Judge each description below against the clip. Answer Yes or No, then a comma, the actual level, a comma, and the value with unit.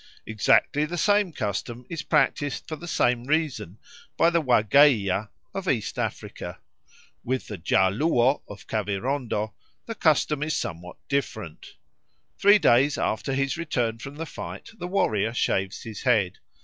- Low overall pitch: Yes, low, 125 Hz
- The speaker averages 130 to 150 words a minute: Yes, average, 145 wpm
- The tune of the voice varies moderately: No, wide, 6.1 semitones